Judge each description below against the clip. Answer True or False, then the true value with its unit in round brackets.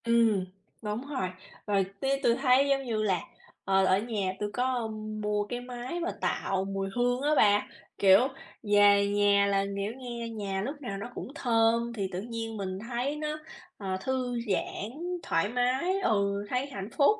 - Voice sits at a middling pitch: False (225 Hz)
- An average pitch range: True (3.9 semitones)